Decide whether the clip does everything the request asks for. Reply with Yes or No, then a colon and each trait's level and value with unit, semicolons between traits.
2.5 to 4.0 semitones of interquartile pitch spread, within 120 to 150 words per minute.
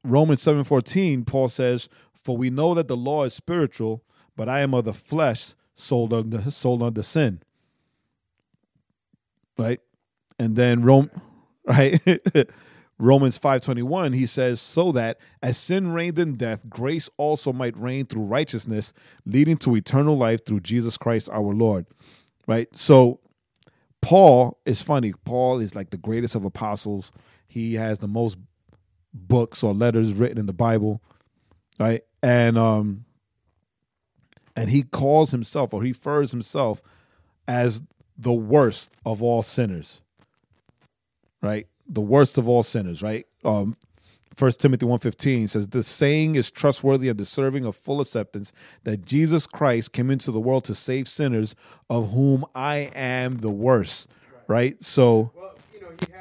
Yes: average, 3.7 semitones; average, 145 wpm